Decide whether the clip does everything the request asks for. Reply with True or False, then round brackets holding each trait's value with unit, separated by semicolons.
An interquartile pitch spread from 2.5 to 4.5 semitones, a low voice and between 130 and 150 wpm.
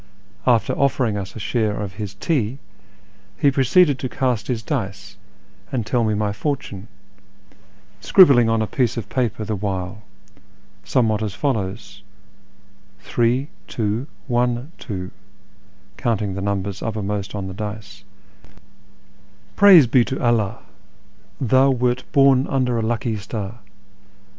True (3.8 semitones; 115 Hz; 140 wpm)